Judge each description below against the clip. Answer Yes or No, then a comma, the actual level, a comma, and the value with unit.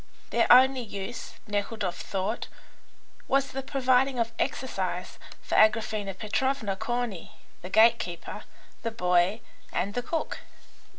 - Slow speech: Yes, slow, 120 wpm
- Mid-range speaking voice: No, high, 225 Hz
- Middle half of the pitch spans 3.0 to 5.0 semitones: Yes, average, 4.0 semitones